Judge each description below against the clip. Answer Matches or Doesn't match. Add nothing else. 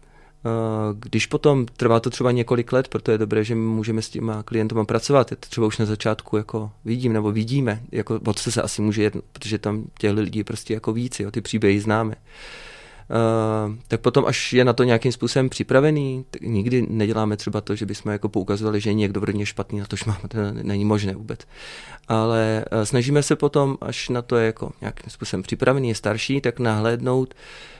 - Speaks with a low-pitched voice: Matches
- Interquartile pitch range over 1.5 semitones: Matches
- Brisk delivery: Matches